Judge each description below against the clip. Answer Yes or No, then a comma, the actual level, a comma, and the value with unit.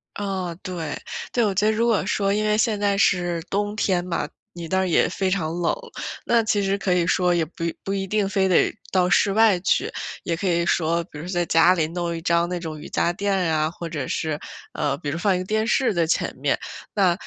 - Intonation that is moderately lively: Yes, average, 3.0 semitones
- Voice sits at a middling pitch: Yes, medium, 180 Hz